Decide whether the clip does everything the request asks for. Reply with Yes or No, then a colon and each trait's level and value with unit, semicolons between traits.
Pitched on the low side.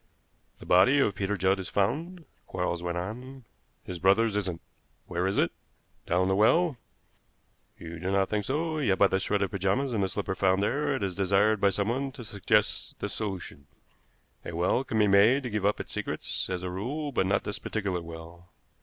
Yes: low, 100 Hz